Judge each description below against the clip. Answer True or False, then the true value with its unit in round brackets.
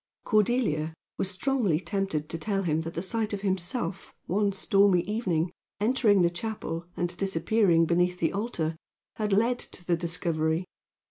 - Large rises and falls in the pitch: False (3.9 semitones)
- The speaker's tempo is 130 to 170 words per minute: True (150 wpm)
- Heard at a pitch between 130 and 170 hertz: False (185 Hz)